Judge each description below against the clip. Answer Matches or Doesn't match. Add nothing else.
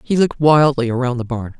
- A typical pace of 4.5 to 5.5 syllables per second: Doesn't match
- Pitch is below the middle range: Matches